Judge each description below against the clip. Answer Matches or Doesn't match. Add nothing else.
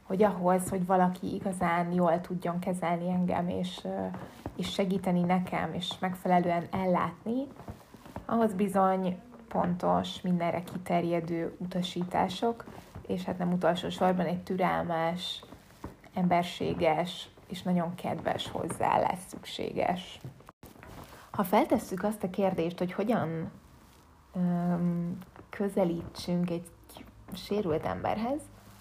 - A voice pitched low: Doesn't match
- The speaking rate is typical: Doesn't match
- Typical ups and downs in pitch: Doesn't match